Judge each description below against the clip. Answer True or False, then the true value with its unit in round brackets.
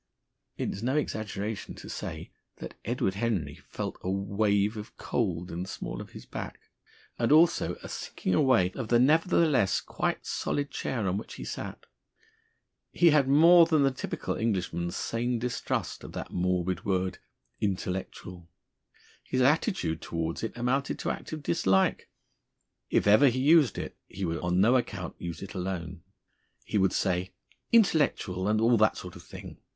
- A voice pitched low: True (105 Hz)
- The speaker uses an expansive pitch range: True (6.0 semitones)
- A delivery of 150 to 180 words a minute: True (160 wpm)